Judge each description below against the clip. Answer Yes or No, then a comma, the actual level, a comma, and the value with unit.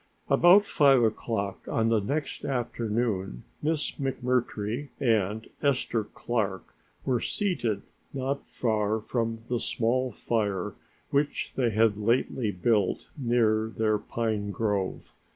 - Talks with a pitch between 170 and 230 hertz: No, low, 115 Hz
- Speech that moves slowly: Yes, slow, 115 wpm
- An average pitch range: Yes, average, 3.4 semitones